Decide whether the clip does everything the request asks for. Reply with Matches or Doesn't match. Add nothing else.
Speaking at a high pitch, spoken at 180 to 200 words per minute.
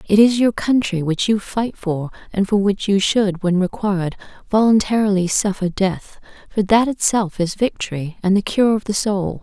Matches